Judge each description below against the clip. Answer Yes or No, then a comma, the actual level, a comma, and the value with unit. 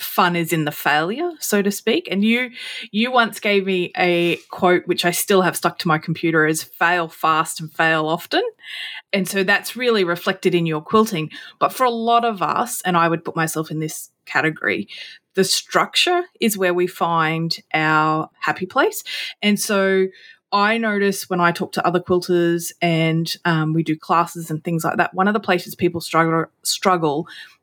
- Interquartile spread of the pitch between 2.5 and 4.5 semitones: Yes, average, 3.9 semitones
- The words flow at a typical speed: Yes, average, 190 wpm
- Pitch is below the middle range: No, medium, 180 Hz